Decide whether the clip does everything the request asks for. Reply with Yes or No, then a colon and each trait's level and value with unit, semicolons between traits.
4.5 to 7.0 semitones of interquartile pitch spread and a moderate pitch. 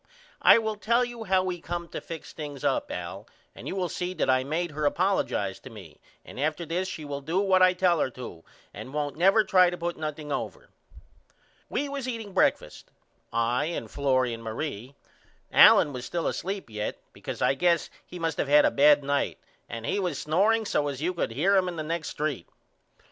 Yes: average, 4.9 semitones; medium, 160 Hz